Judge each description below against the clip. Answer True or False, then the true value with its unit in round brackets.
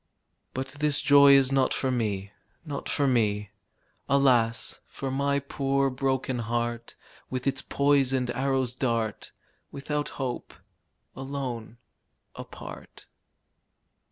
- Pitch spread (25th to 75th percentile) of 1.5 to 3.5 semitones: True (2.7 semitones)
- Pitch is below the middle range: True (130 Hz)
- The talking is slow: True (105 wpm)